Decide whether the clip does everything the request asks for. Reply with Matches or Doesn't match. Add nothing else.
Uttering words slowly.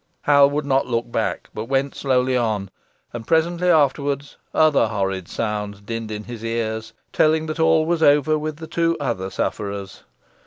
Doesn't match